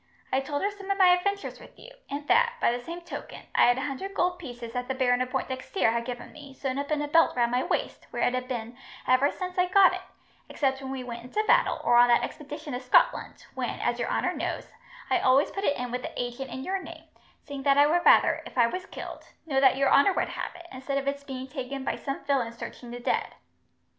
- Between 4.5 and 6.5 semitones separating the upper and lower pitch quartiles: Yes, average, 5.2 semitones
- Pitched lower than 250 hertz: No, very high, 275 Hz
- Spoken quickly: Yes, fast, 255 wpm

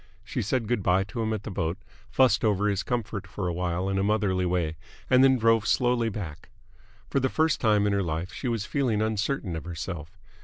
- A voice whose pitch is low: Yes, low, 105 Hz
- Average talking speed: No, fast, 215 wpm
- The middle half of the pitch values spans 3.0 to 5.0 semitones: Yes, average, 4.0 semitones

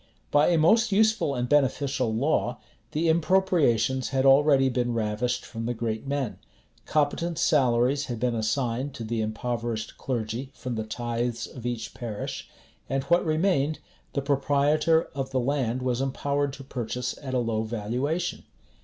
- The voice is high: No, low, 130 Hz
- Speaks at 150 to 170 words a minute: Yes, average, 155 wpm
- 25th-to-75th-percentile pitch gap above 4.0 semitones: No, average, 3.5 semitones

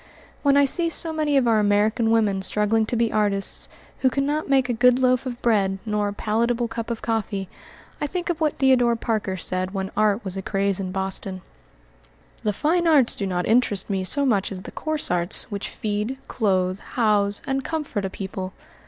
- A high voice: Yes, high, 220 Hz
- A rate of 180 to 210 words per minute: Yes, average, 195 wpm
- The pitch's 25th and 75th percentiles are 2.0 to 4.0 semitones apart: No, average, 4.6 semitones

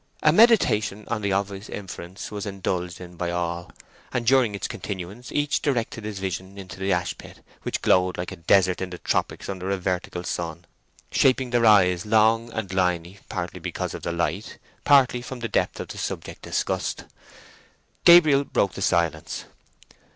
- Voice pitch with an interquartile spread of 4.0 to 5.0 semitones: Yes, average, 4.3 semitones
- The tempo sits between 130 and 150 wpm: No, average, 170 wpm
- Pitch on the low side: Yes, very low, 95 Hz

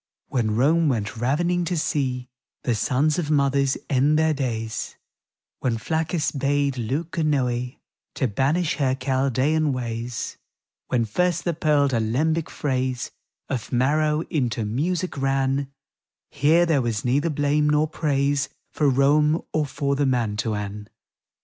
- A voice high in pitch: No, medium, 140 Hz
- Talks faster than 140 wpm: No, slow, 135 wpm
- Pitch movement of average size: Yes, average, 3.4 semitones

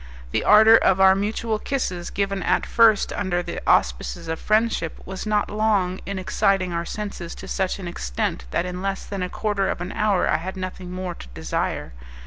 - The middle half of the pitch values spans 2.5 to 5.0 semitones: Yes, average, 2.8 semitones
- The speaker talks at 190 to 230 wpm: Yes, average, 195 wpm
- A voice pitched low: No, high, 190 Hz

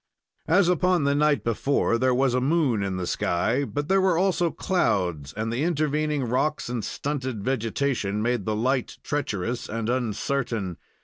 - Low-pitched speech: Yes, low, 130 Hz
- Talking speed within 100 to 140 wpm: No, average, 165 wpm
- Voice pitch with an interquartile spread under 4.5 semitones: No, average, 5.3 semitones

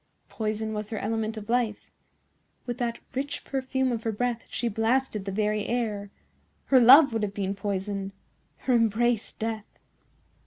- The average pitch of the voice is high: Yes, high, 225 Hz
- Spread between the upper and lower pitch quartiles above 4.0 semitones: No, narrow, 2.6 semitones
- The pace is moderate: Yes, average, 150 wpm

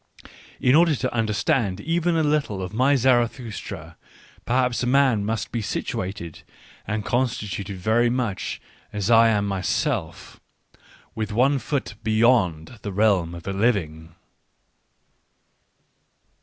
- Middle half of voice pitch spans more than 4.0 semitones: Yes, average, 4.5 semitones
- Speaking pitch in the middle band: No, low, 110 Hz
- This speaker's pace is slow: Yes, slow, 120 wpm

